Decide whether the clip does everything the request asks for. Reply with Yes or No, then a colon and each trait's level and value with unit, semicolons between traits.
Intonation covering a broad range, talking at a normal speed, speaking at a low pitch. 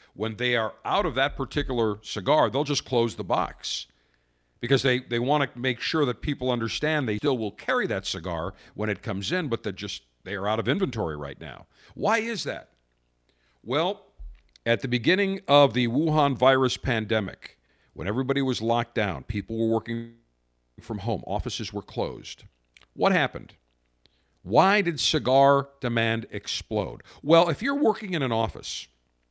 Yes: wide, 6.9 semitones; average, 165 wpm; low, 115 Hz